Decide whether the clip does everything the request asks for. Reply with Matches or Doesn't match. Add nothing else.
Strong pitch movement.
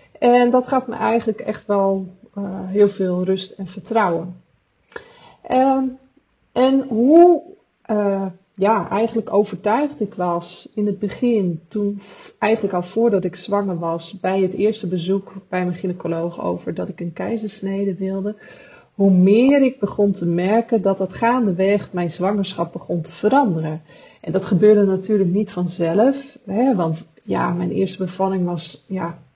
Doesn't match